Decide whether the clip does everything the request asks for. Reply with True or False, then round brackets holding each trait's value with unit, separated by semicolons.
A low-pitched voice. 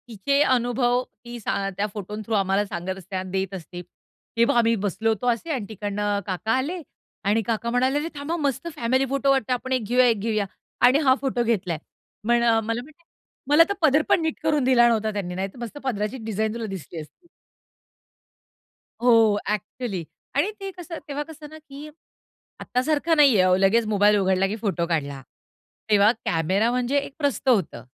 False (230 Hz)